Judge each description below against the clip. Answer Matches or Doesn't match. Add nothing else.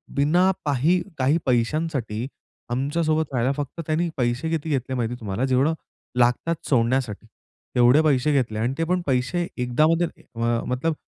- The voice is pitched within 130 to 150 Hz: Matches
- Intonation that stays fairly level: Doesn't match